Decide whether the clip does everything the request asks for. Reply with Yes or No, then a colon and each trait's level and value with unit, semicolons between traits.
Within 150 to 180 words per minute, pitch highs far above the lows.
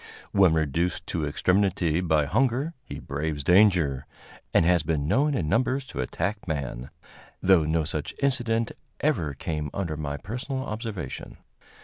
No: average, 140 wpm; wide, 6.1 semitones